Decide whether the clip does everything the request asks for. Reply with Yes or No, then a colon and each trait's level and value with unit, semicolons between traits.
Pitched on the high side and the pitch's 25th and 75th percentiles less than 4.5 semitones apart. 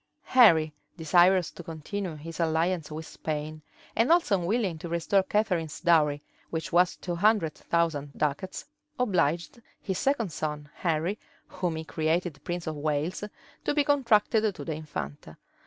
No: medium, 170 Hz; average, 3.7 semitones